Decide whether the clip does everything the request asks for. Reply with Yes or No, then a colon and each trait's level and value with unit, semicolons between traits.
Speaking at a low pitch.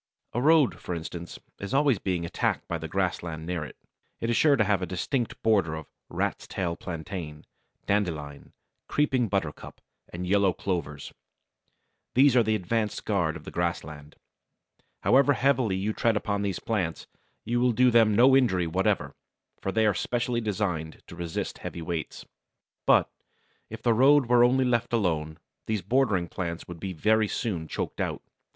Yes: low, 100 Hz